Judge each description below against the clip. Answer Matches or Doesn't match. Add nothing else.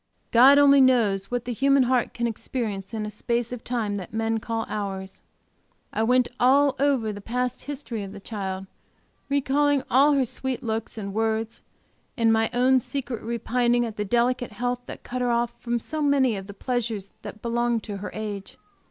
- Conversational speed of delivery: Matches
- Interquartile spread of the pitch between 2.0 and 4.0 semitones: Matches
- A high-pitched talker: Matches